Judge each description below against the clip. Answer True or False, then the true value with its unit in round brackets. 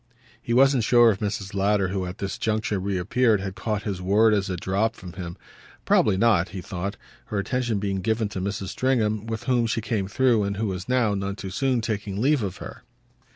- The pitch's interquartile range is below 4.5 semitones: True (2.7 semitones)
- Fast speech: True (210 wpm)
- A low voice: True (105 Hz)